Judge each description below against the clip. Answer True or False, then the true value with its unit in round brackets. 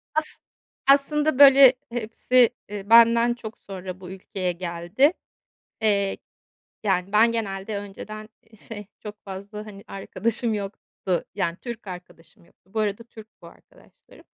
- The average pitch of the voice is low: False (210 Hz)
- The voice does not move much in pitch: False (3.2 semitones)